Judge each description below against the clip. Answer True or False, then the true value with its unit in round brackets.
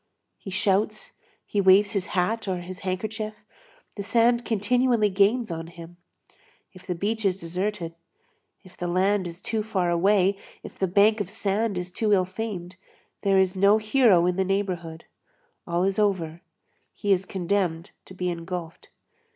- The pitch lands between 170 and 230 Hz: True (190 Hz)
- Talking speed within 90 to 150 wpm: False (160 wpm)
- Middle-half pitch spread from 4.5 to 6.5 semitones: False (2.8 semitones)